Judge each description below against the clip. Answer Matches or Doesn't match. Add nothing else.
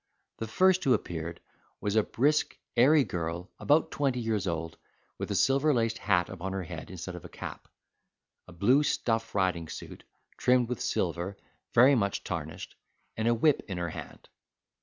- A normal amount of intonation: Doesn't match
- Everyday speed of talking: Matches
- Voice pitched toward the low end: Matches